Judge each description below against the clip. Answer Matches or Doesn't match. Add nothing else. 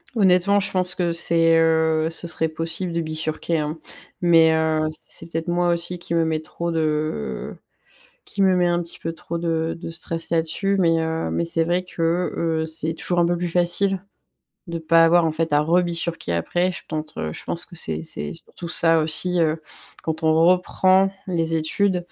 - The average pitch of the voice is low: Doesn't match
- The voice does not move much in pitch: Matches